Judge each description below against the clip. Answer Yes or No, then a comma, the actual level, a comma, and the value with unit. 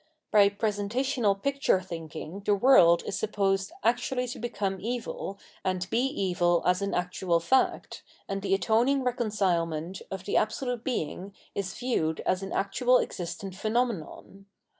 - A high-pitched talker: Yes, high, 200 Hz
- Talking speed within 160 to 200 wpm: No, average, 140 wpm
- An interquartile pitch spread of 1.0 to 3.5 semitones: No, average, 4.4 semitones